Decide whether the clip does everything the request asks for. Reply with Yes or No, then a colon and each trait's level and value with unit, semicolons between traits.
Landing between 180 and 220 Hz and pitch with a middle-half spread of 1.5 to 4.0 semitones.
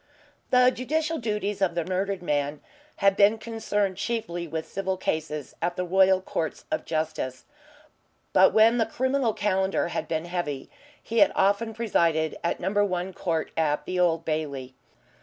No: medium, 185 Hz; average, 4.7 semitones